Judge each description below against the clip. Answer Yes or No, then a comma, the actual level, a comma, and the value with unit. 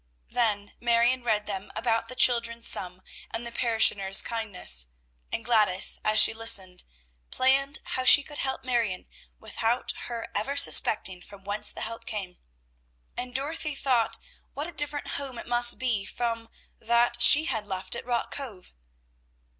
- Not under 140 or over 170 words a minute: Yes, average, 155 wpm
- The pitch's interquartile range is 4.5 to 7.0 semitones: No, average, 3.6 semitones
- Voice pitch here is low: No, high, 230 Hz